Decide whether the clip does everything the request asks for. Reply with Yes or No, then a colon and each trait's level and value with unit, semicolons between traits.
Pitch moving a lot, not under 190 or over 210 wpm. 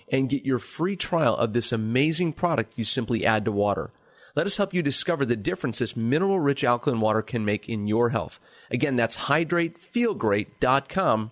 No: wide, 5.8 semitones; average, 180 wpm